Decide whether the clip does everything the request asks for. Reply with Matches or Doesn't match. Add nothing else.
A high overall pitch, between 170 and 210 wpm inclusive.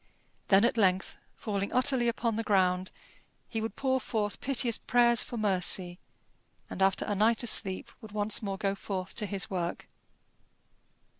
Doesn't match